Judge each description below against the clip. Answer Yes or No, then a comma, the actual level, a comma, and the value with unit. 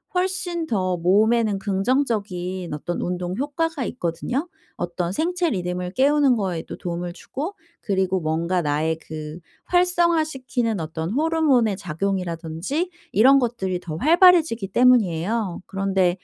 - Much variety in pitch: Yes, wide, 7.8 semitones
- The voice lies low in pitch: No, high, 200 Hz